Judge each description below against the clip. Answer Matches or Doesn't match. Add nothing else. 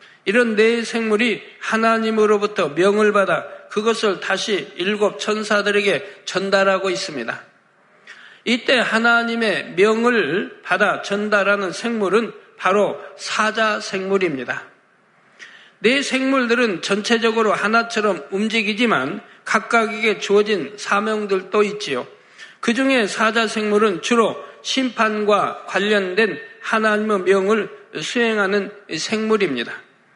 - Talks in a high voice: Matches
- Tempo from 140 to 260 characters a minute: Matches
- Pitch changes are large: Doesn't match